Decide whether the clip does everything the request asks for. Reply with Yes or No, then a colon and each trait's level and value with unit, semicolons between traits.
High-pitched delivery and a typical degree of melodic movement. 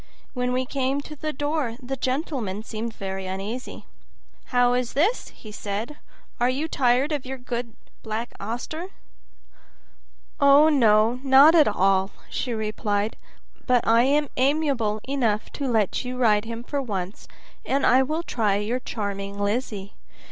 Yes: high, 245 Hz; average, 4.4 semitones